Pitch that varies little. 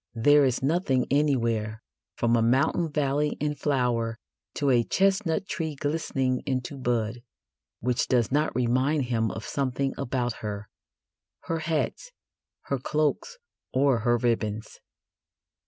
No: average, 3.9 semitones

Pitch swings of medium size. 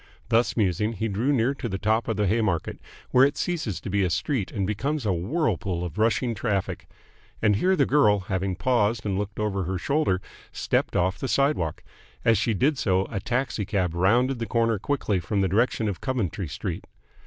Yes: average, 4.5 semitones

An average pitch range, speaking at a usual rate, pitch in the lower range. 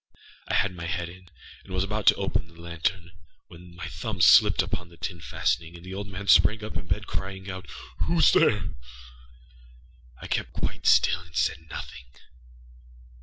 No: narrow, 2.3 semitones; average, 170 wpm; very low, 90 Hz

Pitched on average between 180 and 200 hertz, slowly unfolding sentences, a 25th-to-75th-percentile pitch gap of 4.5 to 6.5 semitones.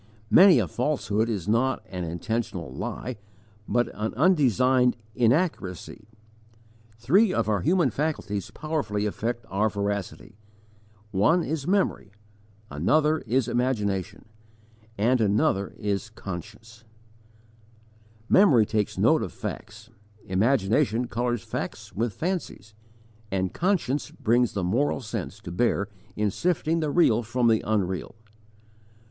No: low, 115 Hz; slow, 115 wpm; average, 5.1 semitones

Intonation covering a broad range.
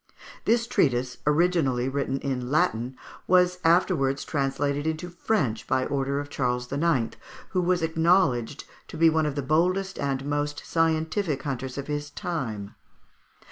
No: average, 3.9 semitones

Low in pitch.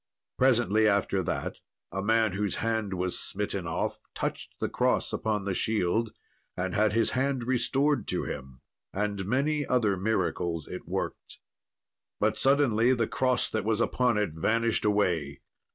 Yes: low, 110 Hz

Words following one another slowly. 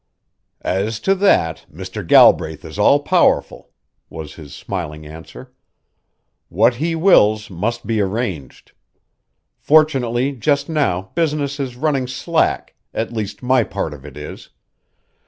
Yes: slow, 125 wpm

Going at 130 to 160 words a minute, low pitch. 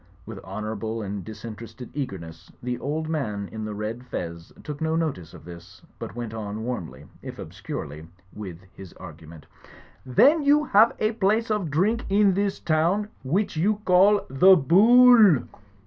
Yes: average, 155 wpm; low, 130 Hz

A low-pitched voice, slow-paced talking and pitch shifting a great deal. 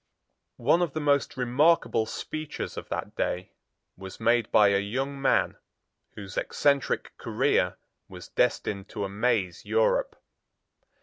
Yes: low, 125 Hz; slow, 125 wpm; wide, 6.4 semitones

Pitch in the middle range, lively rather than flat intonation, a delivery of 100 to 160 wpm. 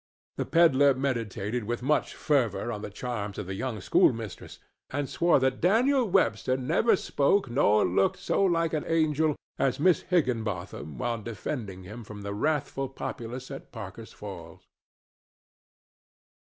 No: low, 130 Hz; wide, 6.3 semitones; average, 140 wpm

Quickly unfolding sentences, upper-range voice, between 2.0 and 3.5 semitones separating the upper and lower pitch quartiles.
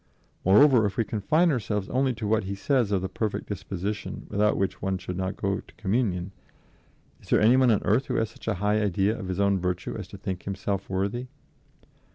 No: fast, 210 wpm; low, 100 Hz; average, 2.8 semitones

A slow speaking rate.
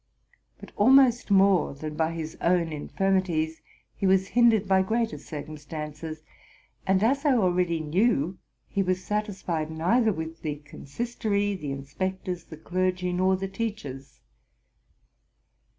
Yes: slow, 125 wpm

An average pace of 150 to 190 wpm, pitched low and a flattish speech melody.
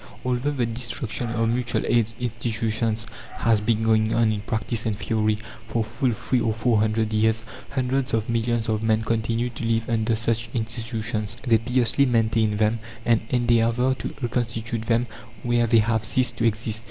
Yes: average, 170 wpm; low, 115 Hz; narrow, 1.3 semitones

